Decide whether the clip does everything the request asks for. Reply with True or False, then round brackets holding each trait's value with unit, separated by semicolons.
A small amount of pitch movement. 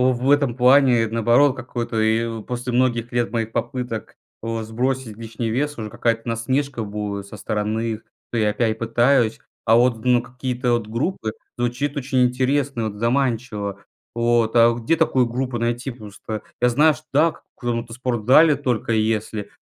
True (2.3 semitones)